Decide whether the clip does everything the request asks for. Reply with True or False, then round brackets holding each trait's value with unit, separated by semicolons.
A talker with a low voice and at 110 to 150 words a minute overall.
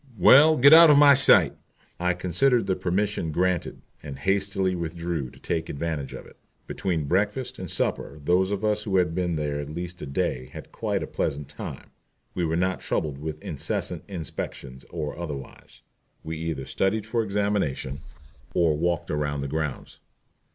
False (85 Hz; 170 wpm)